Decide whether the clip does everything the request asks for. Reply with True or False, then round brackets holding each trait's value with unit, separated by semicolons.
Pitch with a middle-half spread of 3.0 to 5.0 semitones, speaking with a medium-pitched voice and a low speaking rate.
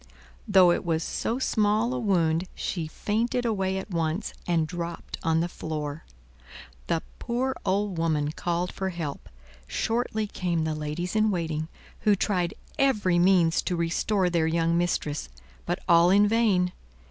False (3.9 semitones; 175 Hz; 150 wpm)